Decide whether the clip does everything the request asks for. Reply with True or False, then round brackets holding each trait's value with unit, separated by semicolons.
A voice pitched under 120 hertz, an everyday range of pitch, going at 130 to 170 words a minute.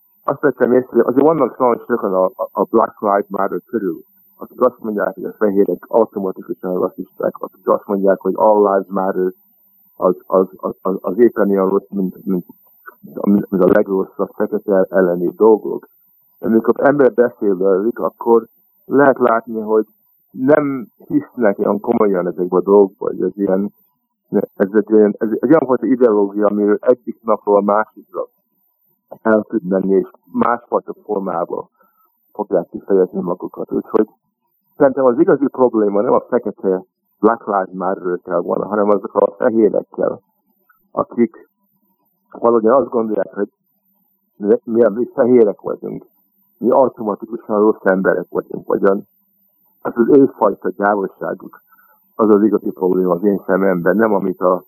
False (110 Hz; 7.4 semitones; 145 wpm)